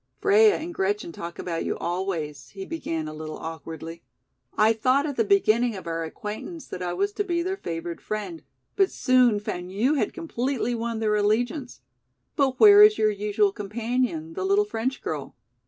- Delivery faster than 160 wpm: Yes, average, 180 wpm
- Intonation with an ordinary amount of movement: No, wide, 7.1 semitones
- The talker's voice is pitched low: No, high, 215 Hz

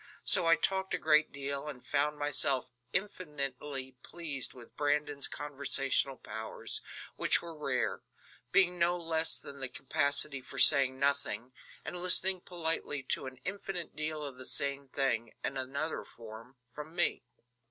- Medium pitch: Yes, medium, 145 Hz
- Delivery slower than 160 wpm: Yes, average, 145 wpm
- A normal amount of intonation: Yes, average, 3.2 semitones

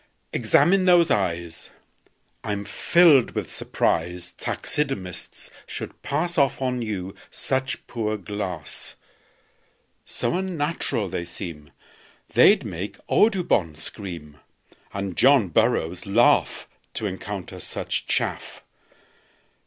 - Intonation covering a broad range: Yes, wide, 7.6 semitones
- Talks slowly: Yes, slow, 100 wpm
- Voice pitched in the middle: No, low, 105 Hz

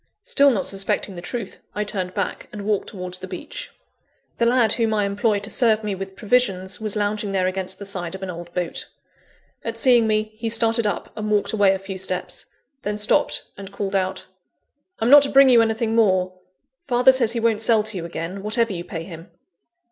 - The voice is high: Yes, high, 205 Hz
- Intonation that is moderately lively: Yes, average, 3.2 semitones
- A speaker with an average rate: No, fast, 210 wpm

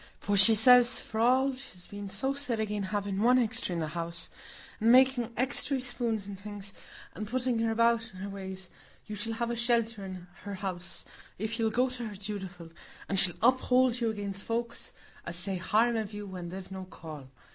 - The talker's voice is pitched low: No, high, 215 Hz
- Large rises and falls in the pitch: No, average, 3.7 semitones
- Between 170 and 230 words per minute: Yes, average, 200 wpm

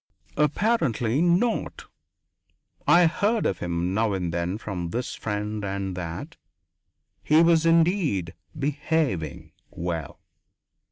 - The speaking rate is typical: No, slow, 105 wpm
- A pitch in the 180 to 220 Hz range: No, low, 110 Hz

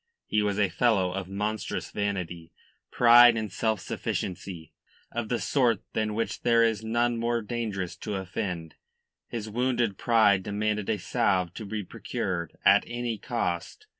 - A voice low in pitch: Yes, low, 105 Hz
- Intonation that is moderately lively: Yes, average, 3.5 semitones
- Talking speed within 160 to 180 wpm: No, average, 150 wpm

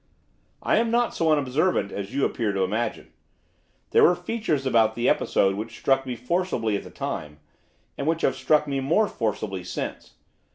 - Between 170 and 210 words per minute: Yes, average, 175 wpm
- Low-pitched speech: Yes, low, 130 Hz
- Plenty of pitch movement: Yes, wide, 6.7 semitones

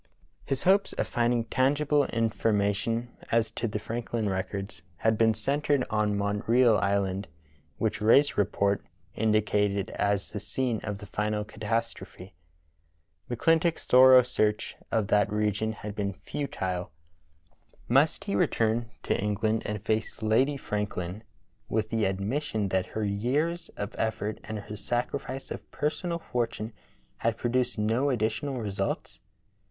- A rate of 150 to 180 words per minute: No, slow, 135 wpm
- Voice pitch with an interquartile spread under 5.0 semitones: Yes, average, 3.0 semitones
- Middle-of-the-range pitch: No, low, 110 Hz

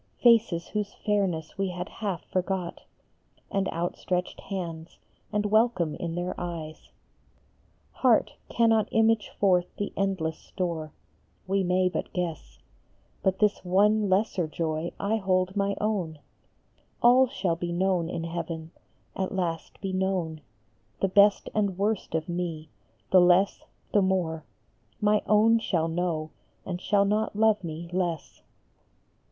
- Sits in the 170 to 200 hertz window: Yes, medium, 185 Hz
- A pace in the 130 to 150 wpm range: Yes, slow, 135 wpm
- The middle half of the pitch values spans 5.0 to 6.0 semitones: No, average, 3.3 semitones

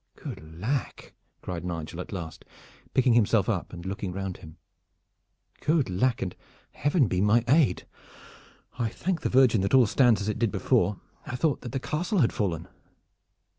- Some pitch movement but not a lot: No, wide, 6.2 semitones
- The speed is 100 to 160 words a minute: No, average, 170 wpm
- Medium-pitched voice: No, low, 110 Hz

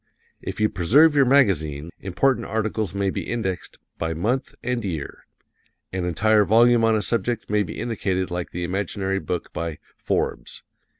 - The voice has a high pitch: No, low, 100 Hz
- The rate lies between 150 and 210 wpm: Yes, average, 160 wpm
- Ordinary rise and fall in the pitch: Yes, average, 4.6 semitones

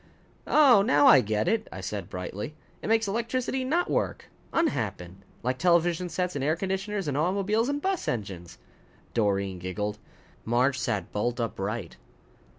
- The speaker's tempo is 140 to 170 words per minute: Yes, average, 150 wpm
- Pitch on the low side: No, medium, 145 Hz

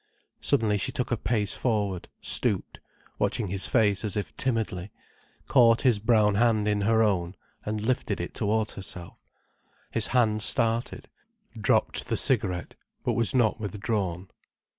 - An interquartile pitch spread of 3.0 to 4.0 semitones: No, narrow, 2.4 semitones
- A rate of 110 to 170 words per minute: Yes, average, 140 wpm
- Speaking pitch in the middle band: No, low, 105 Hz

